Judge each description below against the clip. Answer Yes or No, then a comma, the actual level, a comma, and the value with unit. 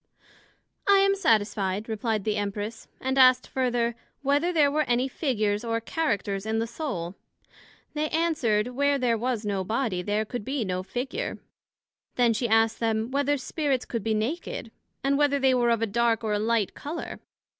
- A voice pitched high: Yes, high, 235 Hz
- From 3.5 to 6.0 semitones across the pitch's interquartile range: Yes, average, 4.3 semitones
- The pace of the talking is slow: No, average, 175 wpm